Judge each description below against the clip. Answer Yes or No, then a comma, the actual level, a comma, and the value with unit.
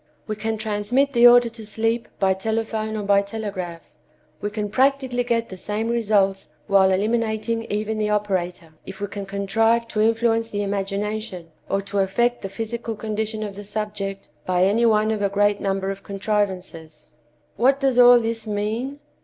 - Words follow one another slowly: No, average, 170 wpm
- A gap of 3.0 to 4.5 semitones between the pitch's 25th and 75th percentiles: No, narrow, 2.4 semitones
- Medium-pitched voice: No, high, 210 Hz